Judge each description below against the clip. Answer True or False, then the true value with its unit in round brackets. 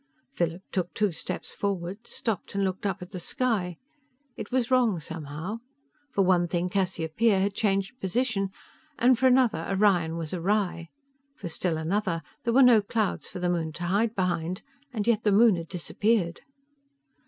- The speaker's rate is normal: True (165 wpm)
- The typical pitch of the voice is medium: False (195 Hz)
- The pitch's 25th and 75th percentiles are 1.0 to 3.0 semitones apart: False (4.0 semitones)